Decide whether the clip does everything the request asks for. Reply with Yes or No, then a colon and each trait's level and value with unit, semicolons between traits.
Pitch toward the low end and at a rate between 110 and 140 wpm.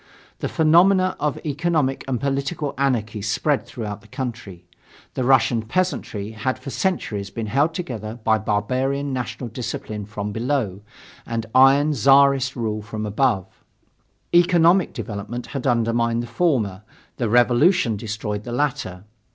Yes: low, 125 Hz; slow, 135 wpm